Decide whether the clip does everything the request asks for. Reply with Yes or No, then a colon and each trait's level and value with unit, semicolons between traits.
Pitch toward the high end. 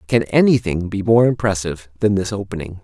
No: low, 100 Hz